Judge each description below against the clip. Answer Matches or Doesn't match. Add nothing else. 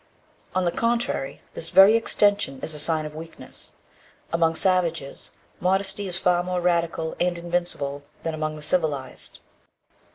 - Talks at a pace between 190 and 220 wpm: Doesn't match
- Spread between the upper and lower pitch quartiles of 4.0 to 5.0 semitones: Doesn't match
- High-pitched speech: Doesn't match